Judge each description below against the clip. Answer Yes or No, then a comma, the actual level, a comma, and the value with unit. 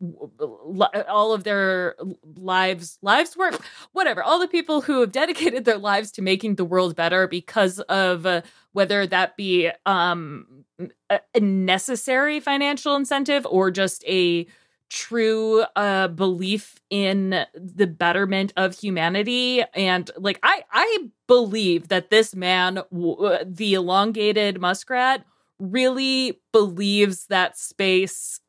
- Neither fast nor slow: No, slow, 120 wpm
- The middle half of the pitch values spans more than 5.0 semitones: No, average, 4.1 semitones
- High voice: Yes, high, 195 Hz